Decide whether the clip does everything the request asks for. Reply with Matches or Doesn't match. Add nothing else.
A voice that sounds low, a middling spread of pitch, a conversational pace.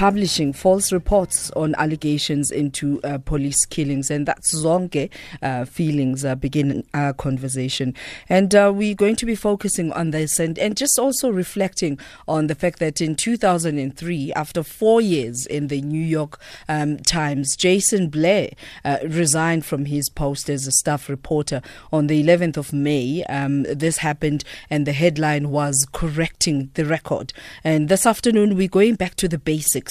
Doesn't match